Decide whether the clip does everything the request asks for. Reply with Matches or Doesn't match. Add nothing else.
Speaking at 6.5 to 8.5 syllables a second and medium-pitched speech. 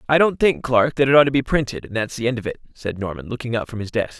Doesn't match